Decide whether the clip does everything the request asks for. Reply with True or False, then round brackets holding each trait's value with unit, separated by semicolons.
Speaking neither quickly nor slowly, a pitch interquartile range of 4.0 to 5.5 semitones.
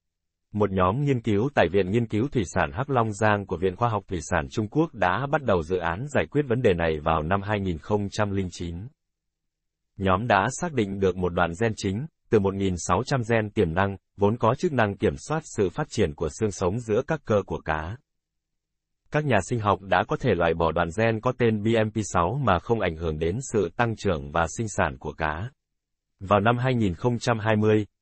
True (205 wpm; 4.5 semitones)